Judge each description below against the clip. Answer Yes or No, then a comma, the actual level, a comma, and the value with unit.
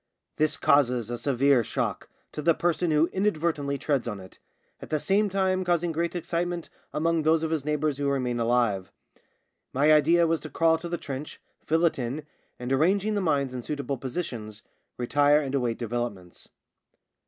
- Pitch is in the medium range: Yes, medium, 150 Hz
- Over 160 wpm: Yes, average, 175 wpm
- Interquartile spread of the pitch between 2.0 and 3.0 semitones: No, average, 4.9 semitones